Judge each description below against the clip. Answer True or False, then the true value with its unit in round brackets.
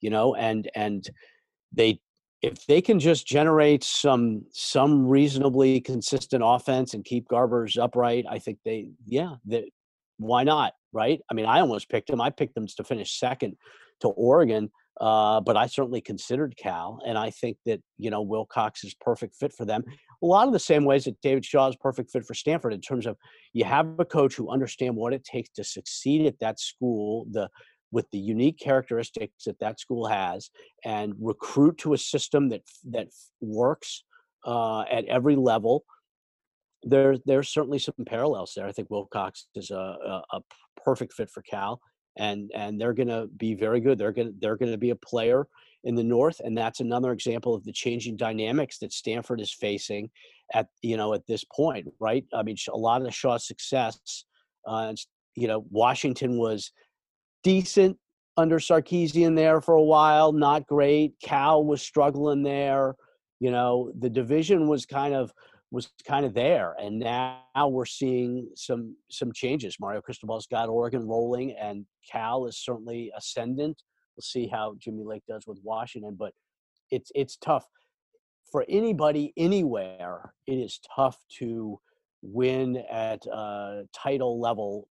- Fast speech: False (170 wpm)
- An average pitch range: True (4.5 semitones)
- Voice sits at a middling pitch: False (125 Hz)